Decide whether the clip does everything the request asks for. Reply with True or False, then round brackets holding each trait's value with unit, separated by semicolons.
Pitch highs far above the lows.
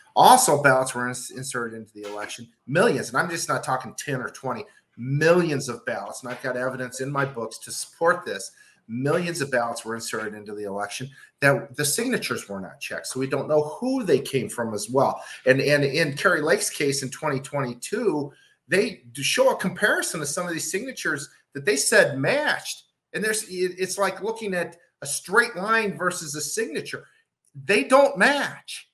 True (6.7 semitones)